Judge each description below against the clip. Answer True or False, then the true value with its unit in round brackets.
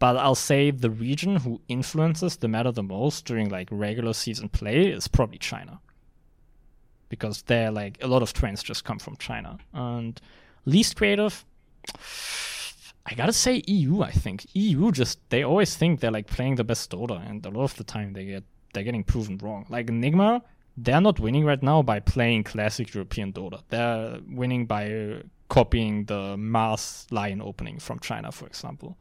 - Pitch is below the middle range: True (120 Hz)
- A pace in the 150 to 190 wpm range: True (180 wpm)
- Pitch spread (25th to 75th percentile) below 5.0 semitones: False (5.4 semitones)